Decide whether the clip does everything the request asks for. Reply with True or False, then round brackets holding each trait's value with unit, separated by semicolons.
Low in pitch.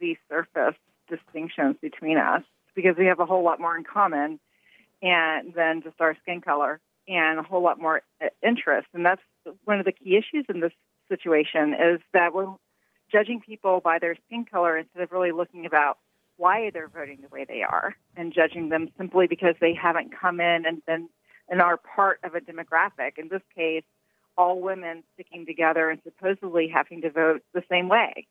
False (170 Hz)